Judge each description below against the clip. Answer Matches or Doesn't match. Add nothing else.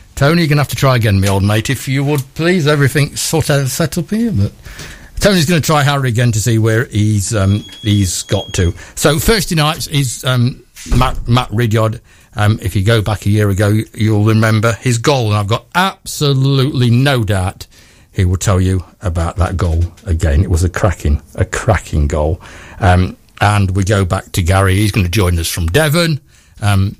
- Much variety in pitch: Matches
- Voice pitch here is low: Matches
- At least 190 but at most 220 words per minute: Matches